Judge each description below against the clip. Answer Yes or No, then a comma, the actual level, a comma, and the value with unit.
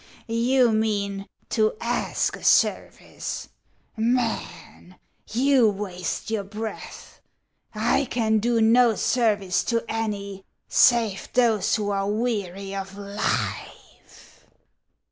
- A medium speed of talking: No, slow, 105 wpm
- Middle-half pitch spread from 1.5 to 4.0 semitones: Yes, average, 2.7 semitones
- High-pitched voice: Yes, high, 220 Hz